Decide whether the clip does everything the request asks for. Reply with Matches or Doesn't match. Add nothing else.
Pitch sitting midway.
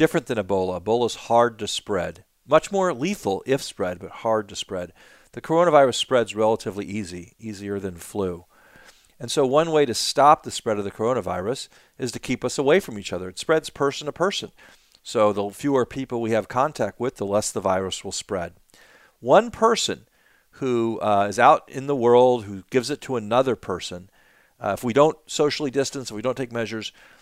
Doesn't match